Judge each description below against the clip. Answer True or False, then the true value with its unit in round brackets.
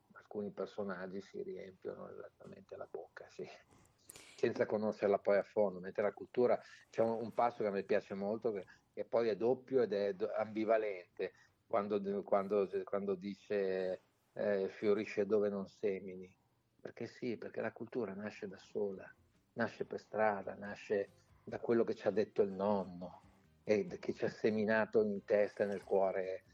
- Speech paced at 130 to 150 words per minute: False (160 wpm)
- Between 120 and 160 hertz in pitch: False (100 Hz)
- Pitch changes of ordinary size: False (1.9 semitones)